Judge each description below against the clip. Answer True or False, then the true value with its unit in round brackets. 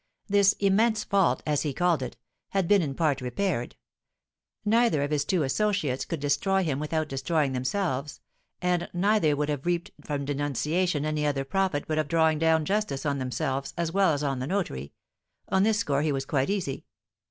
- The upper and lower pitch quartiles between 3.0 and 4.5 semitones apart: False (5.2 semitones)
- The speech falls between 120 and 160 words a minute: False (185 wpm)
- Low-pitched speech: False (155 Hz)